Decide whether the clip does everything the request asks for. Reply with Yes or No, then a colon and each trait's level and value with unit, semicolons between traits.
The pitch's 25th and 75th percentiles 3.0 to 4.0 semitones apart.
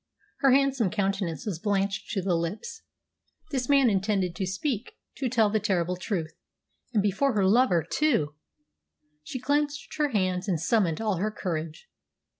No: wide, 5.6 semitones